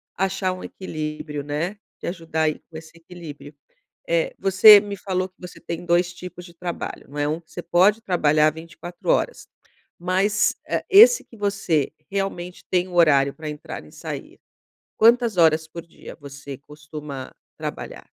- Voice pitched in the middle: Yes, medium, 175 Hz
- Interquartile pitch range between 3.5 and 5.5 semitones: Yes, average, 3.9 semitones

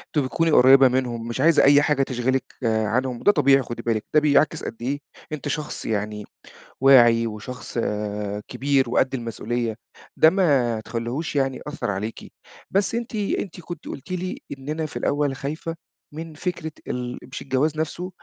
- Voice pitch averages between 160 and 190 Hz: No, low, 135 Hz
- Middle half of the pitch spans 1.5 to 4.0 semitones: No, average, 4.7 semitones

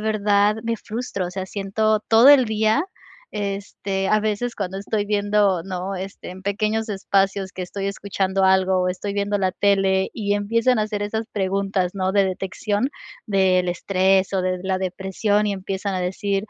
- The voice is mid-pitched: No, high, 200 Hz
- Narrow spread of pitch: Yes, narrow, 1.8 semitones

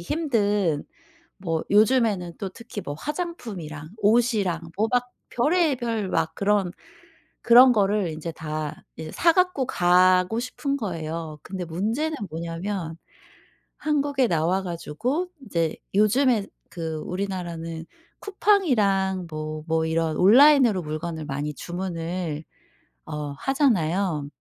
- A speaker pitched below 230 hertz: Yes, high, 190 Hz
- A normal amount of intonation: No, wide, 6.7 semitones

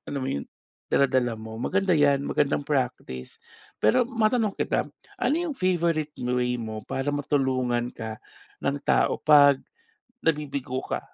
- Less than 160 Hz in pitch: Yes, medium, 140 Hz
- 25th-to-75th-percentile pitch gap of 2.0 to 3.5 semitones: No, average, 4.8 semitones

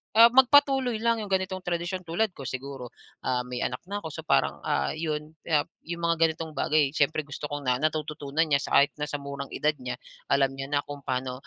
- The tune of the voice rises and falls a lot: No, average, 3.8 semitones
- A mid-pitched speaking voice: Yes, medium, 150 Hz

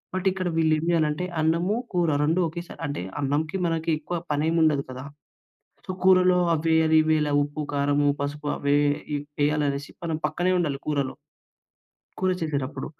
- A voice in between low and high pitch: Yes, medium, 155 Hz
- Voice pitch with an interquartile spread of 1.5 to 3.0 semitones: Yes, average, 2.7 semitones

